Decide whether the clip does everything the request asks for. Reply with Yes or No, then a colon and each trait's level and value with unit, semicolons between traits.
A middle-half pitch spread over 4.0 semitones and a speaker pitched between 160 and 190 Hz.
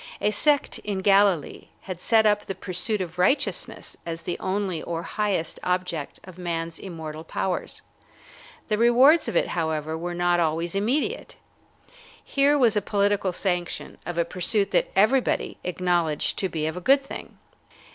No: average, 3.7 semitones; medium, 185 Hz